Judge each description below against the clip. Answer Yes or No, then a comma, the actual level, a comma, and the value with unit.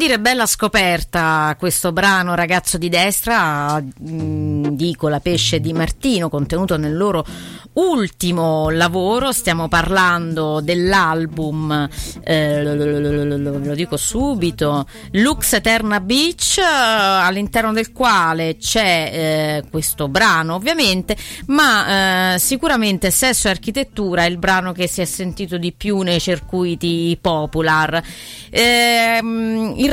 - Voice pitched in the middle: Yes, medium, 180 Hz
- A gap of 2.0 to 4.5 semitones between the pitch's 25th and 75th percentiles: No, wide, 5.4 semitones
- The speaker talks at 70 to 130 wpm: Yes, average, 120 wpm